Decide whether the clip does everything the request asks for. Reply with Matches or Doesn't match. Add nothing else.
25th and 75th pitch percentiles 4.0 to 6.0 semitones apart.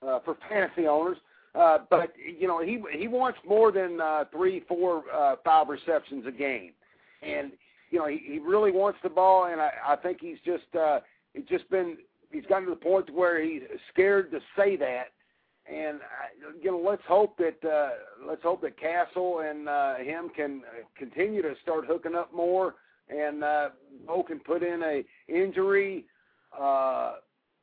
Matches